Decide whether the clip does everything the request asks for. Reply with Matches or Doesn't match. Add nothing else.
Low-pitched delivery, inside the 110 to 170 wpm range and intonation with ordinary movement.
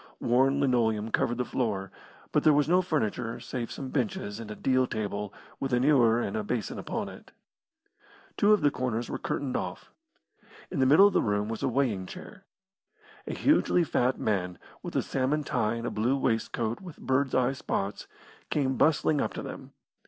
Doesn't match